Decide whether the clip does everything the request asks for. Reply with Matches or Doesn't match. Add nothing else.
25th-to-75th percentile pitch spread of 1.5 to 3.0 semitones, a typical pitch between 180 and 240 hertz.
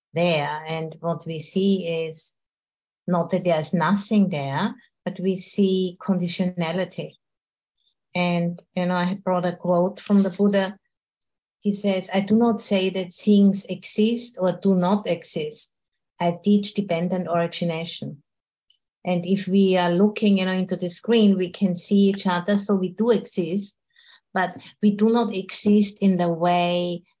Matches